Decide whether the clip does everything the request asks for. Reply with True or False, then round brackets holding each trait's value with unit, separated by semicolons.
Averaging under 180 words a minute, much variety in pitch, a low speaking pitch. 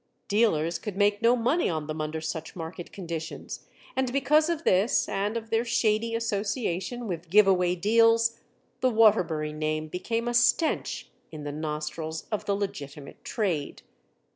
False (155 wpm; 6.3 semitones; 200 Hz)